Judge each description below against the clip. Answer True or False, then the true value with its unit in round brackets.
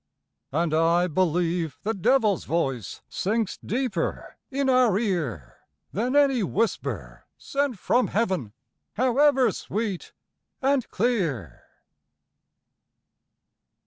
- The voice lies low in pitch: False (205 Hz)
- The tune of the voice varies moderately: False (7.0 semitones)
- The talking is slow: True (90 wpm)